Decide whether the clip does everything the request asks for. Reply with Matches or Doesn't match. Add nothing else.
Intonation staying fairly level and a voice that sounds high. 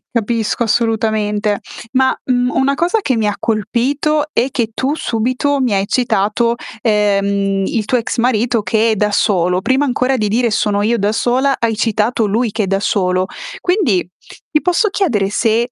Doesn't match